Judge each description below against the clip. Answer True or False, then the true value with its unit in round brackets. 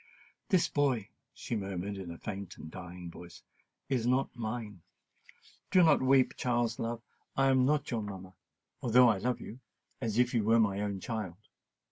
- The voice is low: True (115 Hz)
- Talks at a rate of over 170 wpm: False (155 wpm)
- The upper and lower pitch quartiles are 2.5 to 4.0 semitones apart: False (4.4 semitones)